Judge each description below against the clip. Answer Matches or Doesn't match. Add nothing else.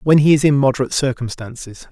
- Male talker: Matches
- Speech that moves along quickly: Doesn't match